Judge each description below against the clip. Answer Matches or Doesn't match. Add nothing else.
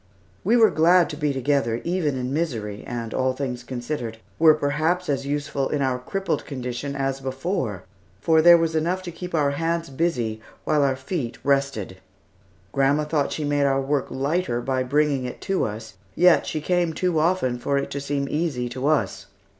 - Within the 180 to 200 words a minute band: Matches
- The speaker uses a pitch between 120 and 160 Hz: Matches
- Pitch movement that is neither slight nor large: Matches